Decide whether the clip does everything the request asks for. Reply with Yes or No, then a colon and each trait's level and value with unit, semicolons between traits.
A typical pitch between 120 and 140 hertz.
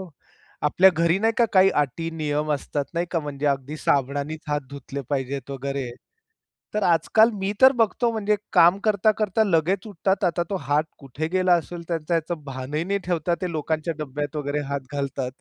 No: medium, 160 Hz